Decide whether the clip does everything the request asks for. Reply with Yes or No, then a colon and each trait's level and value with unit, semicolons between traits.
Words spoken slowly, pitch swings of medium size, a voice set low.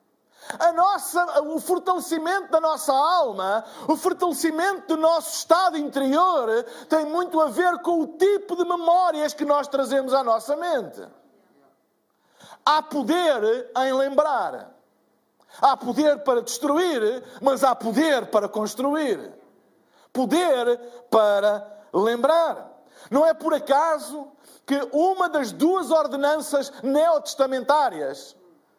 No: slow, 115 wpm; average, 3.8 semitones; very high, 300 Hz